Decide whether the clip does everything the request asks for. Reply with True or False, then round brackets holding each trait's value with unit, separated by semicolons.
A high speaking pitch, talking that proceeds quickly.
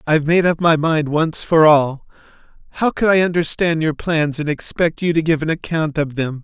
False (160 Hz; 215 wpm)